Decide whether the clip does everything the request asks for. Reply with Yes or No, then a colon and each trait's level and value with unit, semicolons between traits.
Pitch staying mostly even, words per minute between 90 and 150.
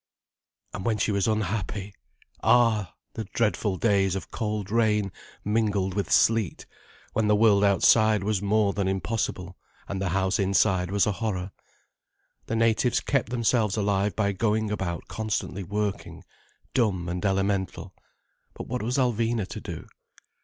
Yes: narrow, 2.3 semitones; average, 145 wpm